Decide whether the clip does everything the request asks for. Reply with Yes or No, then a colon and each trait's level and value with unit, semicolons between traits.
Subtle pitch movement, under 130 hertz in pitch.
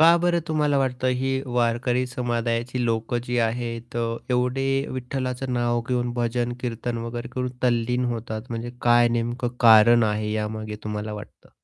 Yes: narrow, 1.4 semitones; low, 120 Hz